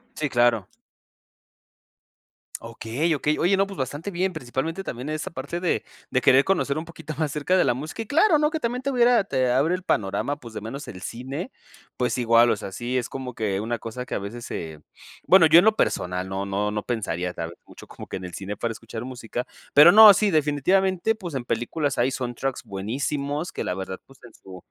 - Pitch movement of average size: No, wide, 6.7 semitones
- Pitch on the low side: Yes, low, 130 Hz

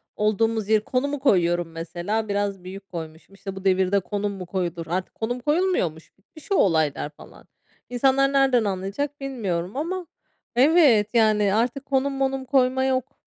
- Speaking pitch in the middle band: No, high, 215 Hz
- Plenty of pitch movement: Yes, wide, 6.1 semitones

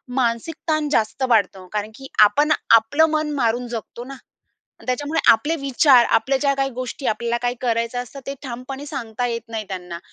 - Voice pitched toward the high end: Yes, high, 245 Hz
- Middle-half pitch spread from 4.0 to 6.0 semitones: No, average, 3.4 semitones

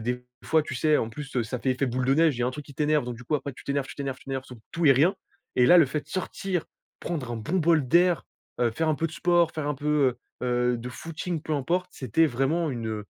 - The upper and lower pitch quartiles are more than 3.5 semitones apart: Yes, average, 4.5 semitones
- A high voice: No, medium, 140 Hz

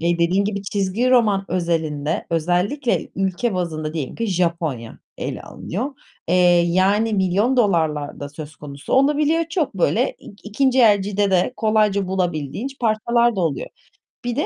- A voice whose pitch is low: No, high, 195 Hz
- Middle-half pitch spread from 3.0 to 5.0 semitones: No, wide, 5.5 semitones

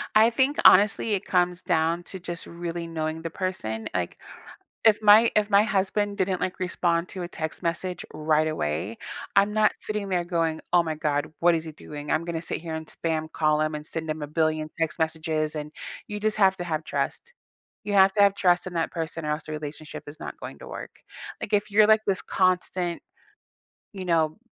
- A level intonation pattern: No, average, 3.5 semitones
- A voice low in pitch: No, medium, 170 Hz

